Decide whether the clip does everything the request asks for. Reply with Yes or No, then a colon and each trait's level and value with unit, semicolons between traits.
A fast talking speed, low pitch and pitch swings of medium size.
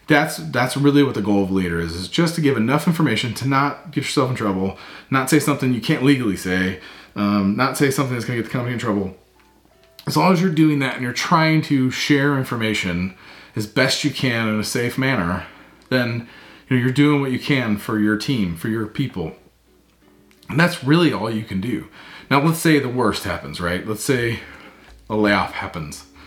No: fast, 215 wpm; low, 125 Hz; wide, 5.7 semitones